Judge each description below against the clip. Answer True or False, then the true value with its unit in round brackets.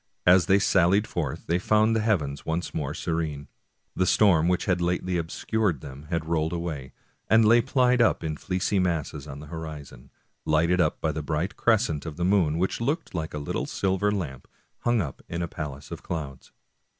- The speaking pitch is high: False (85 Hz)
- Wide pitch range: False (4.2 semitones)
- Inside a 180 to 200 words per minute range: True (195 wpm)